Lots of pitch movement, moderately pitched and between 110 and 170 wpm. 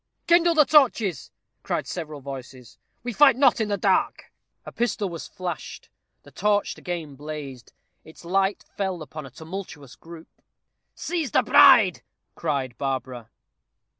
Yes: wide, 7.5 semitones; medium, 175 Hz; slow, 135 wpm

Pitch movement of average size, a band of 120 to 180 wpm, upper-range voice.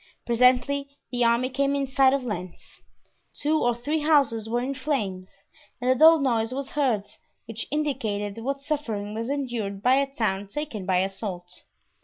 Yes: average, 4.6 semitones; average, 165 wpm; high, 245 Hz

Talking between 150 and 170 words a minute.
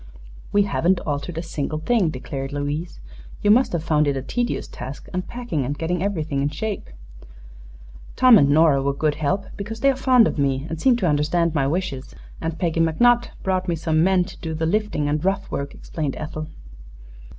No: average, 195 wpm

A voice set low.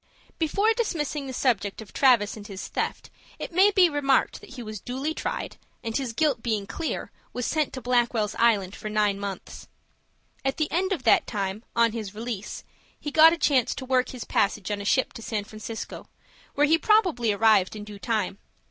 No: high, 235 Hz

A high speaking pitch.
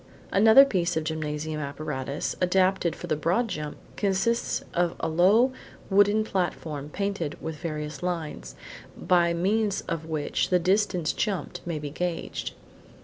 No: medium, 175 Hz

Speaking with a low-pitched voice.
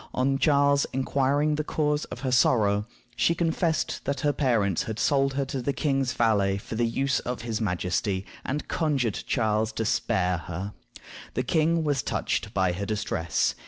Yes: low, 125 Hz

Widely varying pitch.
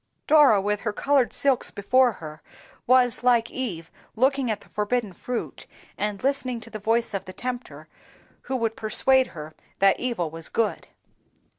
No: average, 4.0 semitones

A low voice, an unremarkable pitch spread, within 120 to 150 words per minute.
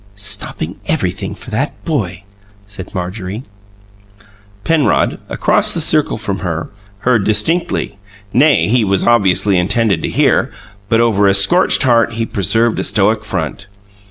Yes: low, 110 Hz; average, 3.6 semitones; slow, 135 wpm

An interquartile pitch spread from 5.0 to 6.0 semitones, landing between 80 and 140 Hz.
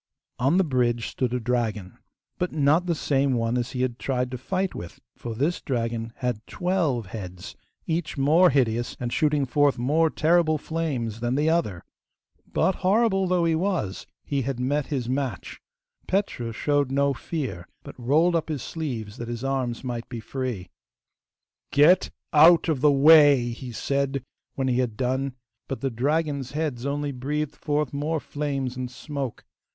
No: average, 4.2 semitones; low, 135 Hz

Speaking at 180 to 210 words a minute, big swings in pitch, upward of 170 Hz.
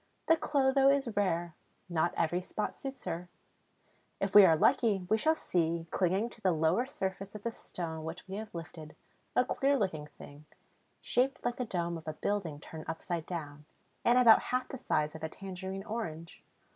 Yes: average, 185 wpm; wide, 6.1 semitones; high, 190 Hz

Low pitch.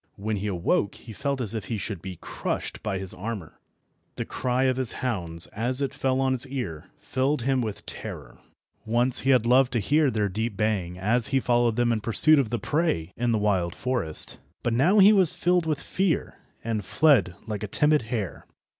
Yes: low, 120 Hz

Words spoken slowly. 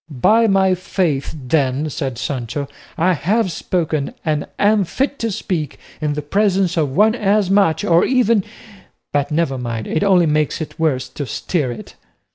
No: average, 165 wpm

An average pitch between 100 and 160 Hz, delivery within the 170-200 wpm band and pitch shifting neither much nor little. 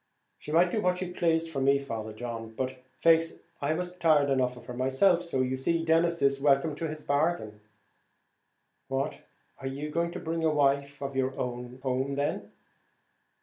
Yes: medium, 140 Hz; average, 185 wpm; average, 3.8 semitones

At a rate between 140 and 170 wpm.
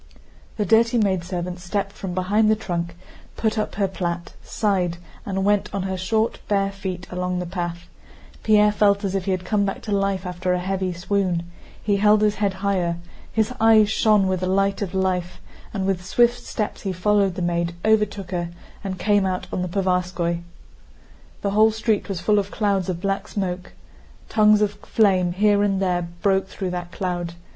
No: average, 185 wpm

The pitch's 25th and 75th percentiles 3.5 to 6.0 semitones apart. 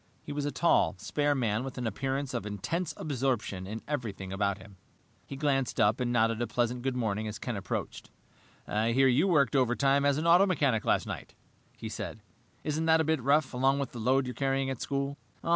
Yes: average, 3.9 semitones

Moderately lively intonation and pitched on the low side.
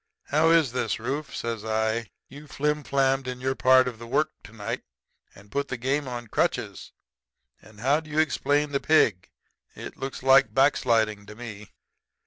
Yes: average, 3.9 semitones; low, 130 Hz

